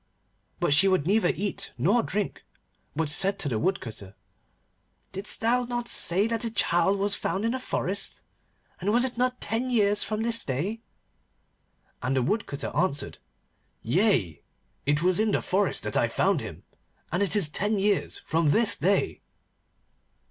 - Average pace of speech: Yes, average, 160 wpm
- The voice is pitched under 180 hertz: No, high, 200 Hz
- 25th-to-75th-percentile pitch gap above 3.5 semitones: Yes, average, 5.0 semitones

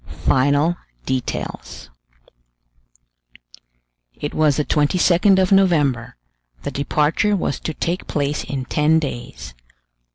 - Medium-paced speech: No, slow, 100 wpm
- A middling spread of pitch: Yes, average, 3.9 semitones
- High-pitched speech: No, medium, 150 Hz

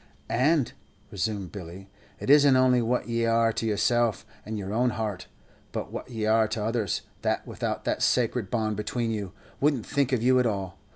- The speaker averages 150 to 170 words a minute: No, average, 185 wpm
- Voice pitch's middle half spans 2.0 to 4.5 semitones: Yes, average, 2.9 semitones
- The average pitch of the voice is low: Yes, low, 115 Hz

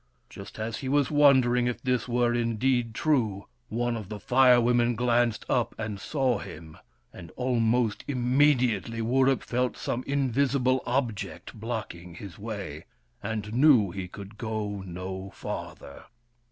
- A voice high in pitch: No, low, 120 Hz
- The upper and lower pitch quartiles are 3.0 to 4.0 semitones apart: Yes, average, 3.4 semitones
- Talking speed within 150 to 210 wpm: No, average, 140 wpm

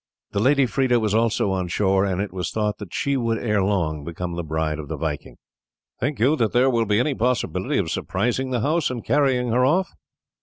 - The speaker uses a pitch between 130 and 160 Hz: No, low, 110 Hz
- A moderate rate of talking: No, fast, 220 wpm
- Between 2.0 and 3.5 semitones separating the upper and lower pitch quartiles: No, wide, 5.5 semitones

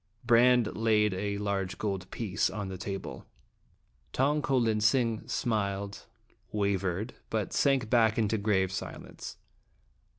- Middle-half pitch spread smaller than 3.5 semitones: Yes, average, 2.8 semitones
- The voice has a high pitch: No, low, 105 Hz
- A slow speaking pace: Yes, slow, 125 wpm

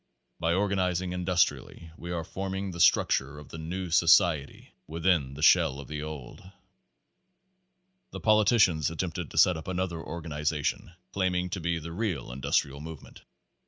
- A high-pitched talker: No, very low, 85 Hz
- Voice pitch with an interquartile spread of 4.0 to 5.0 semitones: No, average, 3.0 semitones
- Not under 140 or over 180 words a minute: Yes, average, 150 wpm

